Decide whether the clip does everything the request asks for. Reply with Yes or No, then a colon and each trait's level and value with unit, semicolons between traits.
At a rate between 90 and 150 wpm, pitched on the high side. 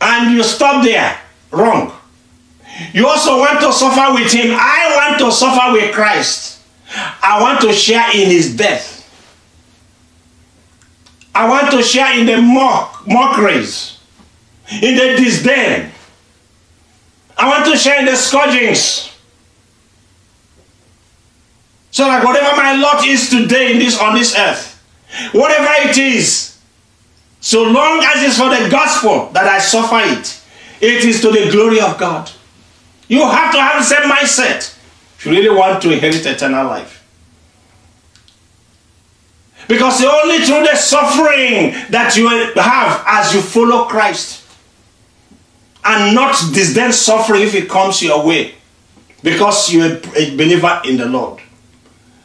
Yes: average, 140 wpm; high, 215 Hz